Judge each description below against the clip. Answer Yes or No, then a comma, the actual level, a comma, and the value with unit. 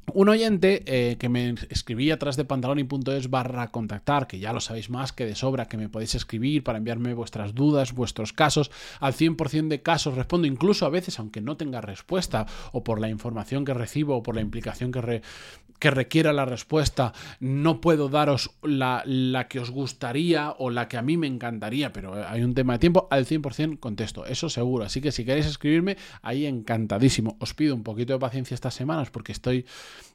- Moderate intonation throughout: Yes, average, 4.0 semitones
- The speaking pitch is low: Yes, low, 130 Hz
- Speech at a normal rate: No, fast, 200 wpm